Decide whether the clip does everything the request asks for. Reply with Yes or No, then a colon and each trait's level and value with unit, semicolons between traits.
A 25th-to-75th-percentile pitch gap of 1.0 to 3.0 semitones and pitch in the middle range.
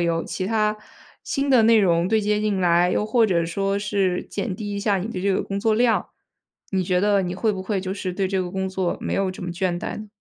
No: narrow, 2.5 semitones; high, 195 Hz